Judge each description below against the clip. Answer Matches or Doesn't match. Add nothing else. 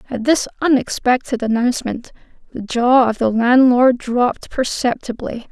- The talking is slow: Matches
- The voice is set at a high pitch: Matches